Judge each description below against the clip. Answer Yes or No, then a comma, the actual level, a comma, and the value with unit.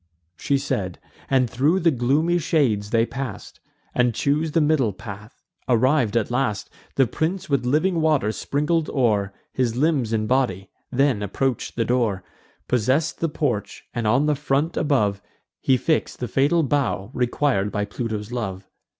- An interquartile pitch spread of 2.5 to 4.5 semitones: No, average, 5.2 semitones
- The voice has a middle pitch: No, low, 130 Hz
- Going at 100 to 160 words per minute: Yes, average, 155 wpm